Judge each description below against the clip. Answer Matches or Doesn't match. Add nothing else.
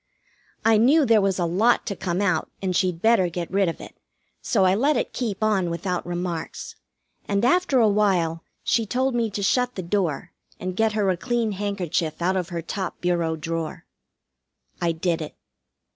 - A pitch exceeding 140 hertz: Matches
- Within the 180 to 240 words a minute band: Matches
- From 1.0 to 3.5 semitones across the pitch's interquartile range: Doesn't match